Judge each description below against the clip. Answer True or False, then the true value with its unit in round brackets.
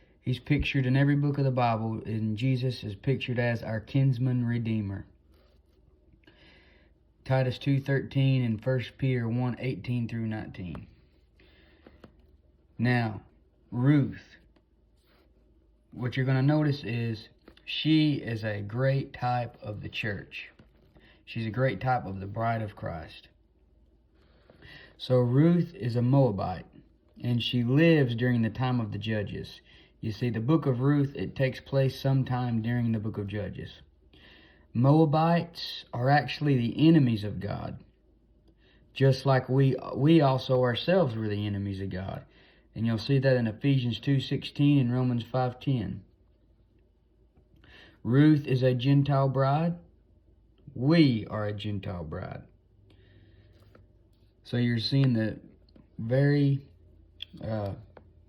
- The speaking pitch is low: True (115 Hz)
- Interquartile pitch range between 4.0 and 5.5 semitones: True (4.7 semitones)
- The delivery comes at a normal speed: False (130 wpm)